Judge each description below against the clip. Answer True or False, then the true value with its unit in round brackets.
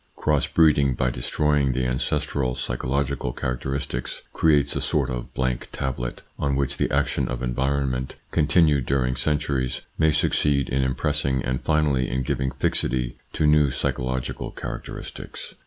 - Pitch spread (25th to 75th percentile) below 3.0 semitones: True (2.4 semitones)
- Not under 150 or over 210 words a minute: False (140 wpm)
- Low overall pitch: True (65 Hz)